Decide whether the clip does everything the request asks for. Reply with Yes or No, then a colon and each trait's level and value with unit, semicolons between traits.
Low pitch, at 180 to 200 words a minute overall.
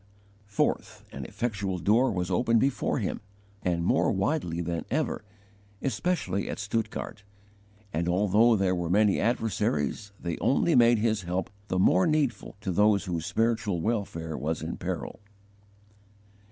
No: low, 100 Hz; average, 140 wpm